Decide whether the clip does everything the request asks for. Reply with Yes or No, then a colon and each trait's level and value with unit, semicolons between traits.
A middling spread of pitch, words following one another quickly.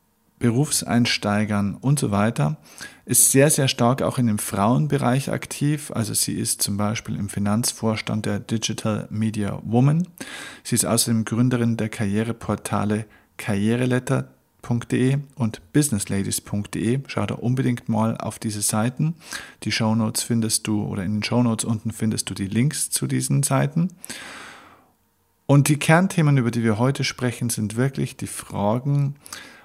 No: average, 4.1 semitones; average, 140 wpm